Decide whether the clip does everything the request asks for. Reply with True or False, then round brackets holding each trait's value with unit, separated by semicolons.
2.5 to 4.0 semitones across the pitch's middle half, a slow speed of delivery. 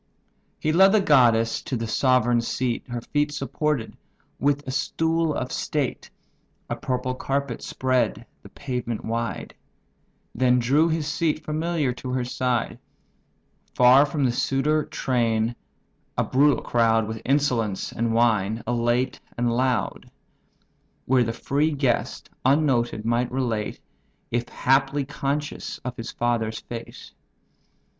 True (3.3 semitones; 130 wpm)